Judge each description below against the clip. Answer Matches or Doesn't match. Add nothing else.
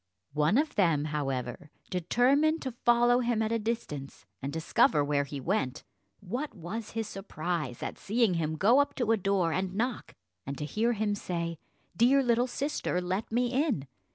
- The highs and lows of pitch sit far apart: Matches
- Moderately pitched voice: Doesn't match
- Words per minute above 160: Matches